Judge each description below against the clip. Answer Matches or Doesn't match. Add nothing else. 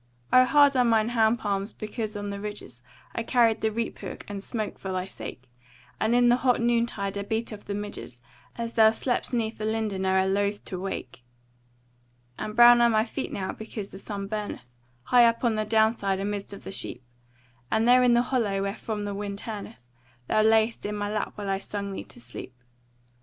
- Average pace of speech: Doesn't match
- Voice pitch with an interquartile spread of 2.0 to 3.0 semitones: Matches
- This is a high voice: Matches